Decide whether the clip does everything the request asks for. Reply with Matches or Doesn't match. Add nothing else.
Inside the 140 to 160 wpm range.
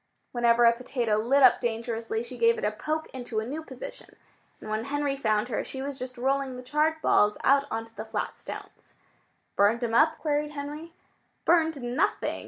Doesn't match